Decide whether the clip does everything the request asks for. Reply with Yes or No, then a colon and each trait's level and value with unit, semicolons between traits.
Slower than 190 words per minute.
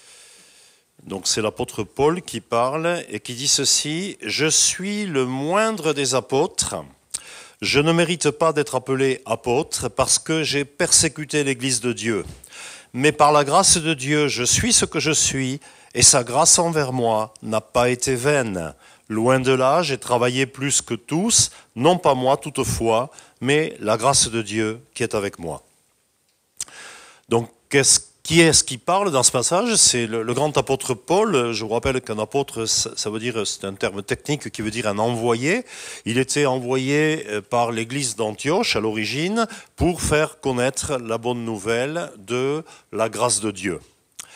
Yes: average, 165 wpm